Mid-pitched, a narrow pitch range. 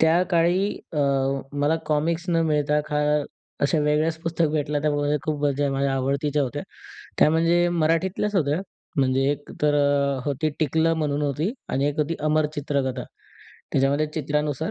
Yes: medium, 150 Hz; narrow, 2.2 semitones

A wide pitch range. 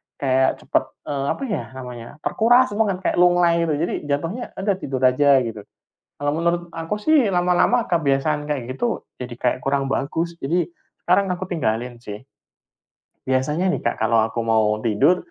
Yes: wide, 5.8 semitones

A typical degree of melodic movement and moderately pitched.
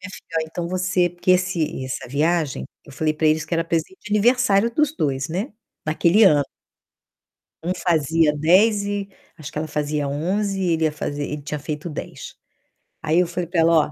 Yes: average, 3.8 semitones; medium, 165 Hz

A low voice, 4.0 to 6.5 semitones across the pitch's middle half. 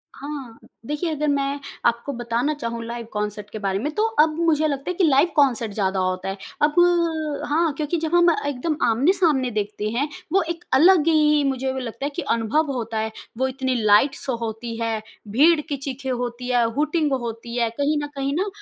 No: very high, 265 Hz; average, 4.6 semitones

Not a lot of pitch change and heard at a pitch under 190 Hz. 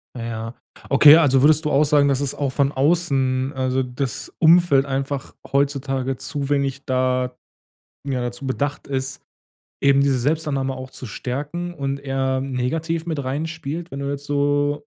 Yes: narrow, 1.8 semitones; medium, 140 Hz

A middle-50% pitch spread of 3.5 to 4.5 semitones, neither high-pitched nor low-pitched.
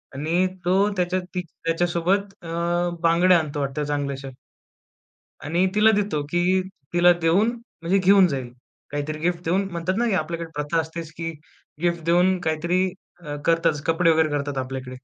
No: average, 3.0 semitones; medium, 170 Hz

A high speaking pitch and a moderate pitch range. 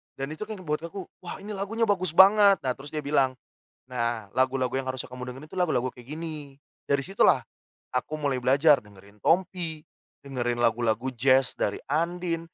No: medium, 140 Hz; average, 4.9 semitones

